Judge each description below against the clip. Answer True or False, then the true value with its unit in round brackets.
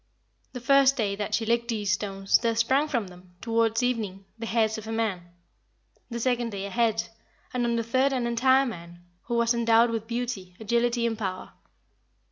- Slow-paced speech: False (190 wpm)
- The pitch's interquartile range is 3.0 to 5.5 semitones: False (2.4 semitones)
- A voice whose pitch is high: True (230 Hz)